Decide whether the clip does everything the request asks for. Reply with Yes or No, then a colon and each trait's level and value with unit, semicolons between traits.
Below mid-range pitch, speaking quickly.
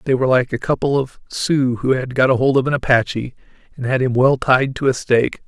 Yes: low, 130 Hz; fast, 240 wpm